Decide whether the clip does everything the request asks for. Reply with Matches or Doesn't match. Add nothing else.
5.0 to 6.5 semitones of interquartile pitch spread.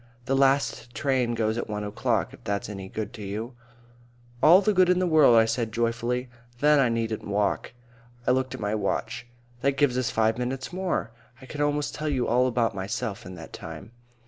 Doesn't match